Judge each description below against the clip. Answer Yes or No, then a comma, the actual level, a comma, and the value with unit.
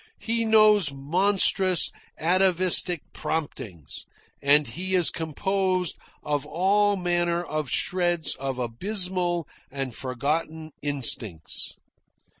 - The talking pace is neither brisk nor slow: No, slow, 90 wpm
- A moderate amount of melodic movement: Yes, average, 4.6 semitones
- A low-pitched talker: No, medium, 170 Hz